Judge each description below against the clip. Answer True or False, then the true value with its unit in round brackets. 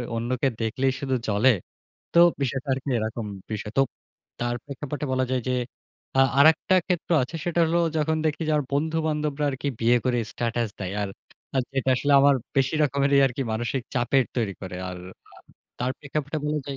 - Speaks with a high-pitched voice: False (135 Hz)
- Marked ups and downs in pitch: False (3.6 semitones)